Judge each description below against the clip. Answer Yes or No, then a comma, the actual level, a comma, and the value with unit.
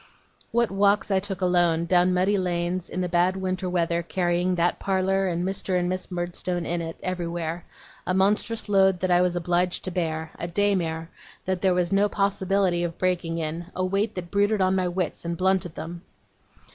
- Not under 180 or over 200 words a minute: Yes, average, 190 wpm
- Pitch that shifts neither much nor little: No, narrow, 1.7 semitones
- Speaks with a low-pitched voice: No, medium, 180 Hz